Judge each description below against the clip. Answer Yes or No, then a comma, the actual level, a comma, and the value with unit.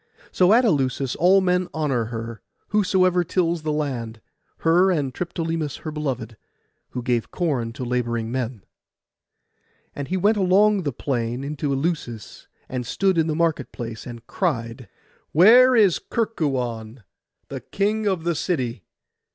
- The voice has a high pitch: No, medium, 150 Hz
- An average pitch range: No, wide, 6.9 semitones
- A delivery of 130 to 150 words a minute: Yes, average, 145 wpm